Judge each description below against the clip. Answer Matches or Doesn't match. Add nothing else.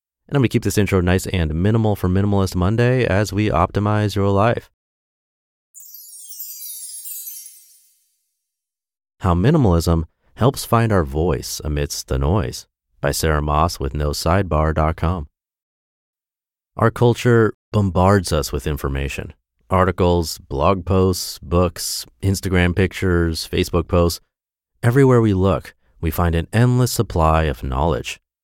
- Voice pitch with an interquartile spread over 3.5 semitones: Matches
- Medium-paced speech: Doesn't match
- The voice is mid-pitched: Doesn't match